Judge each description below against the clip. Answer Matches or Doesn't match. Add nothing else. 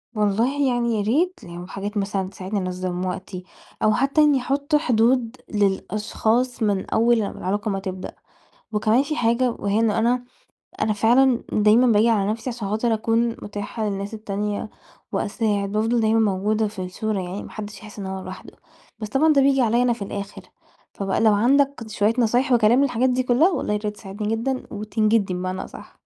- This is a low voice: Doesn't match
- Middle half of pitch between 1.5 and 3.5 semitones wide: Matches